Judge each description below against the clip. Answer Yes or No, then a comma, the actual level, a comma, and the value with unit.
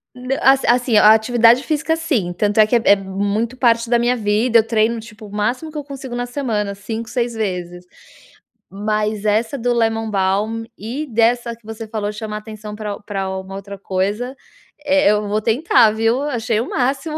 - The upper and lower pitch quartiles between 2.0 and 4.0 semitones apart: Yes, average, 2.7 semitones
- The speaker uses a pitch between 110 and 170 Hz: No, high, 225 Hz